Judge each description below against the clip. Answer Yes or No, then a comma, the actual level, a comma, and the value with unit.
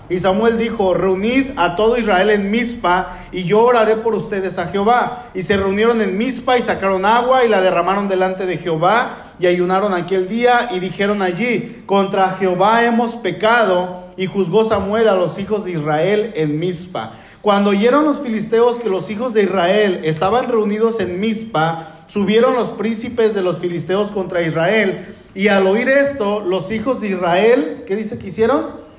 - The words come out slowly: No, average, 175 wpm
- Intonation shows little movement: No, average, 3.6 semitones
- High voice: Yes, high, 200 Hz